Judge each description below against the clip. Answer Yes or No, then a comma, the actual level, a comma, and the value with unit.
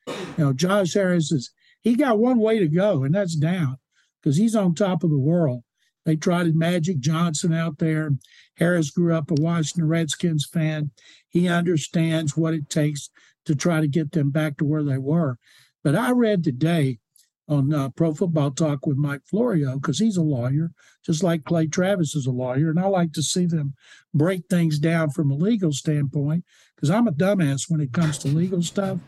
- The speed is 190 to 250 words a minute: Yes, average, 195 wpm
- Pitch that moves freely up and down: No, average, 2.8 semitones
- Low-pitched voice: No, medium, 160 Hz